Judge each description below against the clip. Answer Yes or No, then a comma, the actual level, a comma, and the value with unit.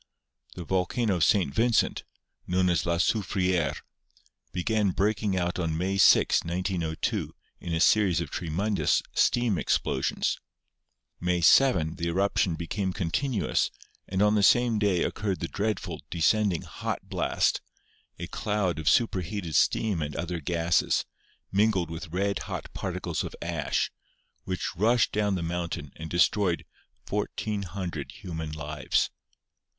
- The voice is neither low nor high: No, very low, 90 Hz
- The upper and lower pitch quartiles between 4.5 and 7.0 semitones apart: No, average, 3.5 semitones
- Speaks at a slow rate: Yes, slow, 130 wpm